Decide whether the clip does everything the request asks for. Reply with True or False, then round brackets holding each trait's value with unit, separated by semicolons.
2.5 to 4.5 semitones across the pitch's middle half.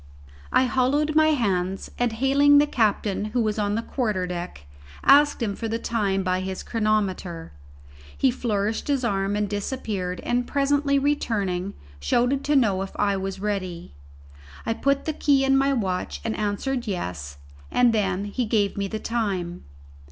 False (5.3 semitones)